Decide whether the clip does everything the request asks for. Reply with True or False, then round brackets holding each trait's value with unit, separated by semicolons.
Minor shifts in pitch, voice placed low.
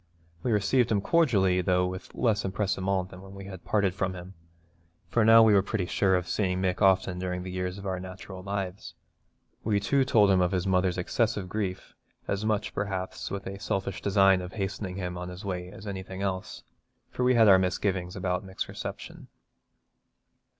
True (1.7 semitones; 95 Hz)